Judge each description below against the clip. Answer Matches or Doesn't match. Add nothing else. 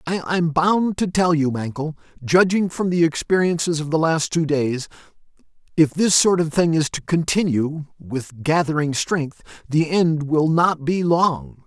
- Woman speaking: Doesn't match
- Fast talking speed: Doesn't match